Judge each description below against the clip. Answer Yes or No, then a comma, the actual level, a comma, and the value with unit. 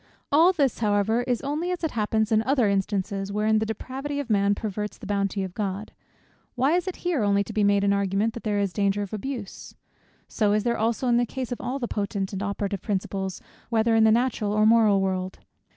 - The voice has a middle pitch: No, high, 215 Hz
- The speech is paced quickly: Yes, fast, 220 wpm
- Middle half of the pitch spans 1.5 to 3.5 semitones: Yes, average, 3.2 semitones